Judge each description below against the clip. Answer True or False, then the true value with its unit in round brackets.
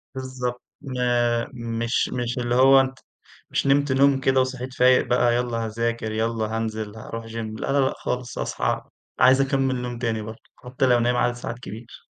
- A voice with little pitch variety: True (2.0 semitones)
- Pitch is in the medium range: False (125 Hz)